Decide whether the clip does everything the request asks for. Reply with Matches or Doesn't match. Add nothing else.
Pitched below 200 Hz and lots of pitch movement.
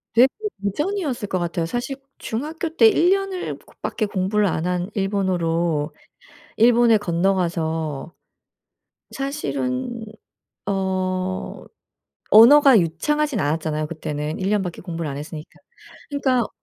Matches